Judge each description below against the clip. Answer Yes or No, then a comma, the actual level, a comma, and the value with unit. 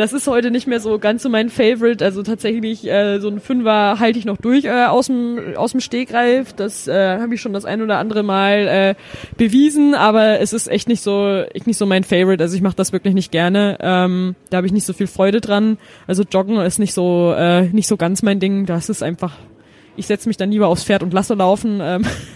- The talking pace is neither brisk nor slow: No, fast, 235 wpm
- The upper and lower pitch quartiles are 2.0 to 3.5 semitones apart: Yes, average, 3.0 semitones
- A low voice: No, high, 205 Hz